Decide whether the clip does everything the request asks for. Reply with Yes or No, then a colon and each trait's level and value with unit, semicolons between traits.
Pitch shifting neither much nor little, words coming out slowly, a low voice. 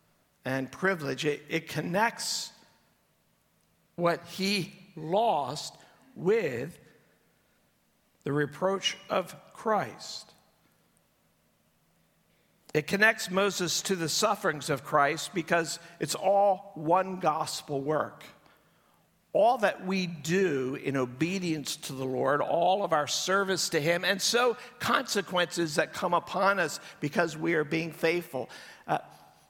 No: average, 4.1 semitones; slow, 110 wpm; medium, 170 Hz